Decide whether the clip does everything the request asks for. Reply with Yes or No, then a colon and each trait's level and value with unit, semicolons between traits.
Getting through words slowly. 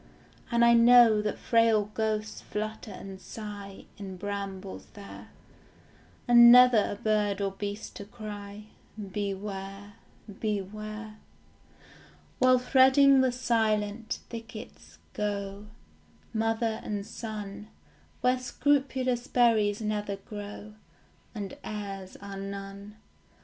Yes: slow, 100 wpm